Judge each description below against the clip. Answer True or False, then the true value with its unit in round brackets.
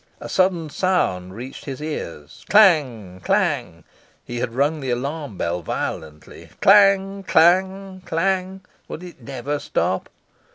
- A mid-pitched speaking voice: True (150 Hz)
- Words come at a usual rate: False (125 wpm)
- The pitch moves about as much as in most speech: False (7.8 semitones)